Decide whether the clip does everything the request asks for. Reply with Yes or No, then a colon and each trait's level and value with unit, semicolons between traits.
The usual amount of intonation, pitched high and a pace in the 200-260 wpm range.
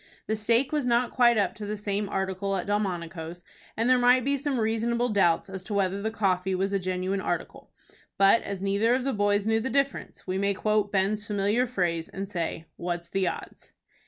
Yes: average, 3.1 semitones; high, 205 Hz; fast, 205 wpm